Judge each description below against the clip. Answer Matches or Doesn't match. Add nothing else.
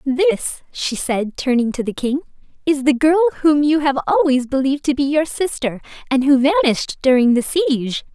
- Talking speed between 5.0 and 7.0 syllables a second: Matches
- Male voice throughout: Doesn't match